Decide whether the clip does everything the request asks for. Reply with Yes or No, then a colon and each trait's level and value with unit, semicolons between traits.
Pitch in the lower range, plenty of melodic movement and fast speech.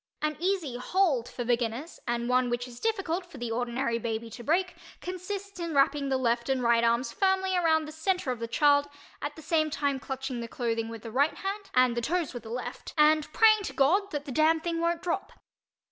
No: very high, 285 Hz; wide, 6.0 semitones; fast, 220 wpm